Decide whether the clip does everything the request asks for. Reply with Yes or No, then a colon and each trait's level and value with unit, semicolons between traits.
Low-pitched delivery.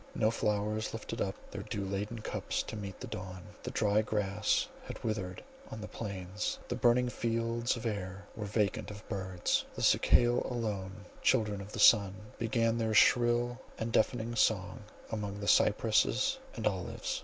Yes: low, 105 Hz